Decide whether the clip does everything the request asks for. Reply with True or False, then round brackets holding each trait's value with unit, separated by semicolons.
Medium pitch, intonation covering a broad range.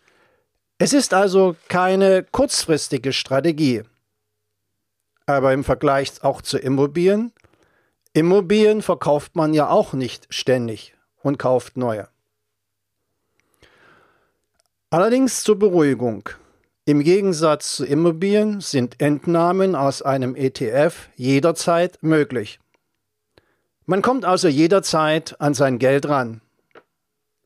True (145 Hz; 6.2 semitones)